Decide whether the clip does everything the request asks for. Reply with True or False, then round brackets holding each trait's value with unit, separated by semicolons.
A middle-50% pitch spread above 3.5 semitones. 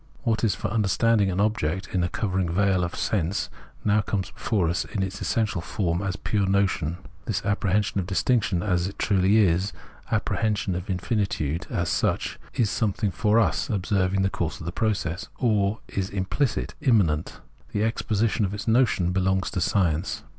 False (2.9 semitones)